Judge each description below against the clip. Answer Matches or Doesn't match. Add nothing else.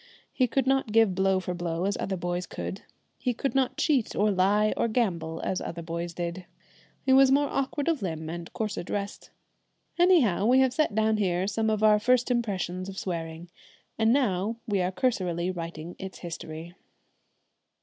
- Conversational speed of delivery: Matches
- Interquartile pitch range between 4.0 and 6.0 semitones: Matches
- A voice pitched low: Doesn't match